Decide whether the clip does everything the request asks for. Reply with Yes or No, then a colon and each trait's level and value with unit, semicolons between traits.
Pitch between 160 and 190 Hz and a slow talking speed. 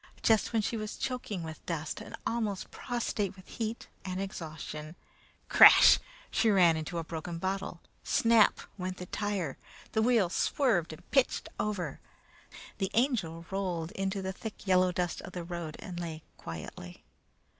No: medium, 185 Hz; average, 155 wpm